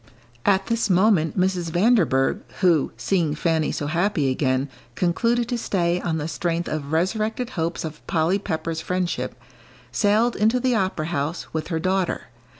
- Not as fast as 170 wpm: Yes, average, 155 wpm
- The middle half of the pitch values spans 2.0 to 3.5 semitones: No, average, 4.2 semitones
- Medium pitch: Yes, medium, 175 Hz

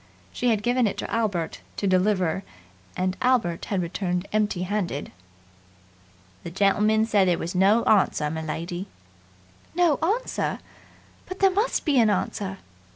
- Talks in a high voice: Yes, high, 200 Hz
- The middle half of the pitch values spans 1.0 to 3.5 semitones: No, average, 4.2 semitones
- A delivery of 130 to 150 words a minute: Yes, average, 140 wpm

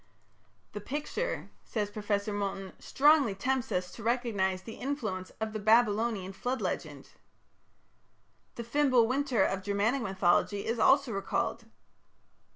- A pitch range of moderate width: Yes, average, 4.0 semitones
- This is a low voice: No, high, 220 Hz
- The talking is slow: Yes, slow, 125 wpm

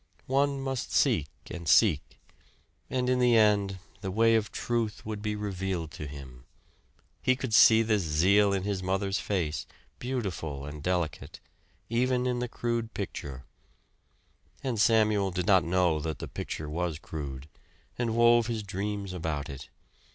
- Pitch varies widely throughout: Yes, wide, 5.8 semitones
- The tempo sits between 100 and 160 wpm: Yes, average, 150 wpm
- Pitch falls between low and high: No, low, 100 Hz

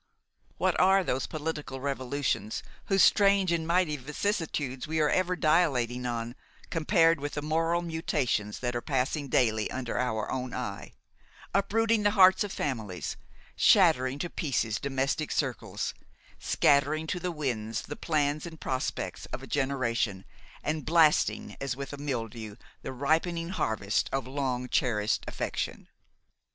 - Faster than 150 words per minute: No, average, 140 wpm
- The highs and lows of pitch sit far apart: No, average, 4.8 semitones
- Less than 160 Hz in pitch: Yes, medium, 140 Hz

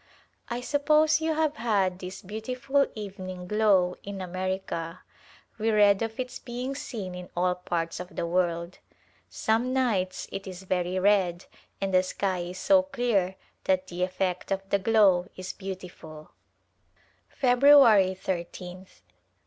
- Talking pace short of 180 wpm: Yes, average, 140 wpm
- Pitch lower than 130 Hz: No, high, 190 Hz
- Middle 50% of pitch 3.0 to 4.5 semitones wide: Yes, average, 3.9 semitones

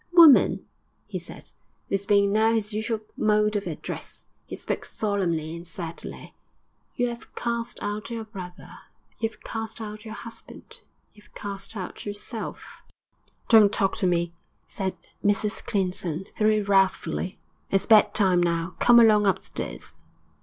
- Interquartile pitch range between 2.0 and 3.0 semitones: Yes, average, 2.7 semitones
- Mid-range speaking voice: No, high, 205 Hz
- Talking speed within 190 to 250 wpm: No, average, 145 wpm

